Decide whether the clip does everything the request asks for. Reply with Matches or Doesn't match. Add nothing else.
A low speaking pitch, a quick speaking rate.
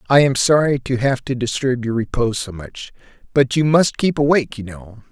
Matches